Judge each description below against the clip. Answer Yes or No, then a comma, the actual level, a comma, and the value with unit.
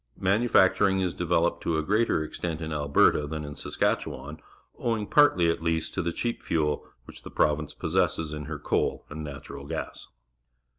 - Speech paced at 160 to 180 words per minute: Yes, average, 170 wpm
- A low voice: Yes, very low, 80 Hz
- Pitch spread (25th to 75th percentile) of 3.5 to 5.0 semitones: Yes, average, 3.8 semitones